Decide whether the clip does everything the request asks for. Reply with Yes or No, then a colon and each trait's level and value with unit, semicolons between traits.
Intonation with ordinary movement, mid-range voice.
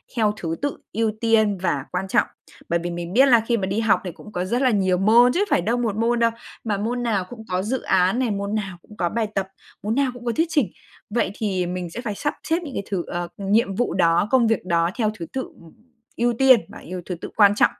No: average, 4.5 semitones; high, 210 Hz